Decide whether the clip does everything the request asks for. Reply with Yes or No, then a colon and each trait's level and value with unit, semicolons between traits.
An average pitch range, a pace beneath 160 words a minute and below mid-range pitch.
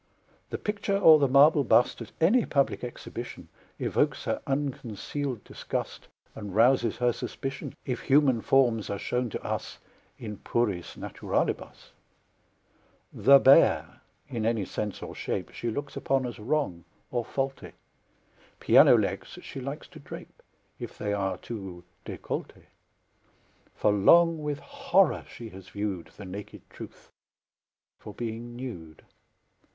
Yes: average, 4.9 semitones; slow, 135 wpm; low, 120 Hz